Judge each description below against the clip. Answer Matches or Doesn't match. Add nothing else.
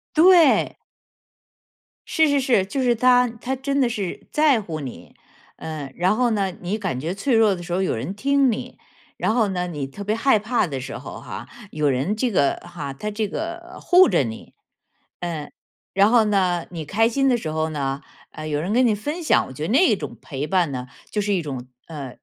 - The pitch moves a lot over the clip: Matches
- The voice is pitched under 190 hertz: Doesn't match